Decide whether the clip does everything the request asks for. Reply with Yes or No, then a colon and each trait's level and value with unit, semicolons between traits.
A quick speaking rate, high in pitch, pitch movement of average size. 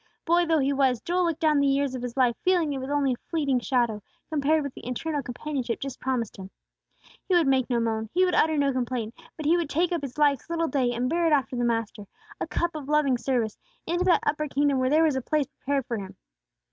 Yes: fast, 250 wpm; very high, 275 Hz; average, 4.0 semitones